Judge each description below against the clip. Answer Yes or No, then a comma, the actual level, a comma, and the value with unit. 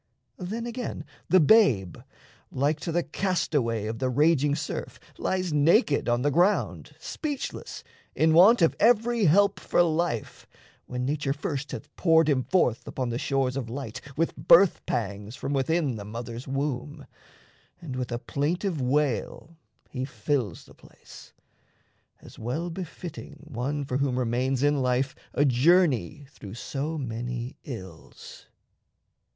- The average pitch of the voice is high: No, medium, 140 Hz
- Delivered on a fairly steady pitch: No, average, 5.1 semitones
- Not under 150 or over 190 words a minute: No, average, 140 wpm